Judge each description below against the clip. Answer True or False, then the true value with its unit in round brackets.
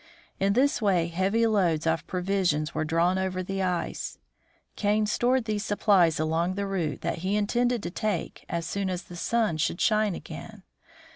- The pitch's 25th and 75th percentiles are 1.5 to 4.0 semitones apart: True (3.7 semitones)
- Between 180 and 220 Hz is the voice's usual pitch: True (190 Hz)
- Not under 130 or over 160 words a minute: False (170 wpm)